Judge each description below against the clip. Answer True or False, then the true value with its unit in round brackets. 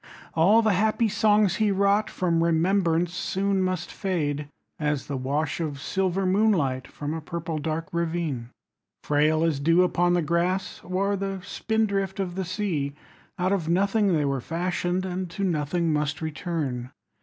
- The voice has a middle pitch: True (175 Hz)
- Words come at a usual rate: True (160 wpm)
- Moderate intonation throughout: True (3.8 semitones)